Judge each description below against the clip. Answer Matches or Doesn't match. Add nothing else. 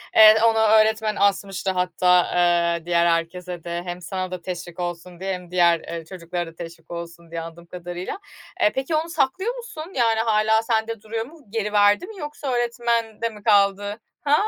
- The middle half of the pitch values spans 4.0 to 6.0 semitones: Matches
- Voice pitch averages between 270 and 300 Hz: Doesn't match